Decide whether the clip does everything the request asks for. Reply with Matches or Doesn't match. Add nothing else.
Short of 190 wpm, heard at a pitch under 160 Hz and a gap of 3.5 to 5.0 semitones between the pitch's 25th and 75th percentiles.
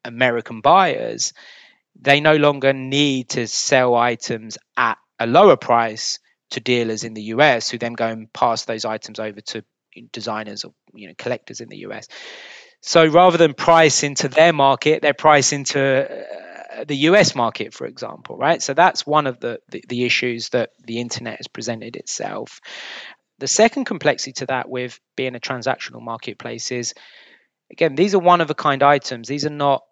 Matches